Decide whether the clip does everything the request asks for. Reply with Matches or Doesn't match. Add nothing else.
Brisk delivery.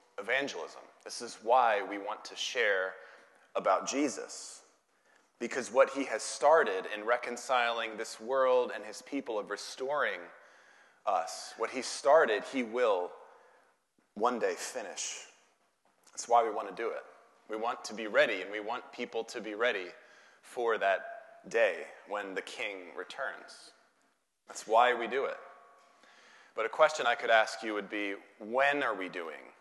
Doesn't match